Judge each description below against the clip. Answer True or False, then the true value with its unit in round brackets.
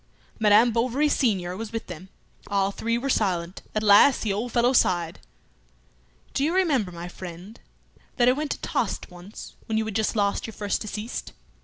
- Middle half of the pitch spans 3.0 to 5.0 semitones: True (4.0 semitones)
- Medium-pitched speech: False (215 Hz)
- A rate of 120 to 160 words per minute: False (180 wpm)